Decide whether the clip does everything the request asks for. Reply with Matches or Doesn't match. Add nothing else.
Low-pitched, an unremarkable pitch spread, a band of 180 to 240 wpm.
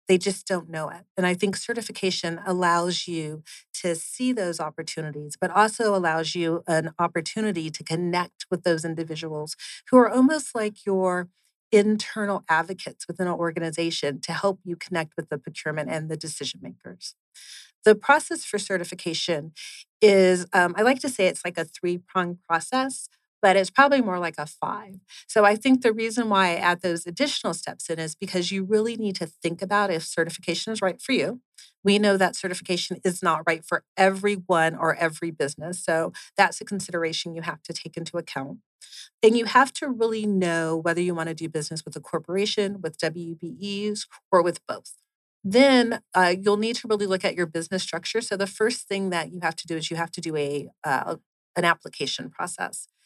Doesn't match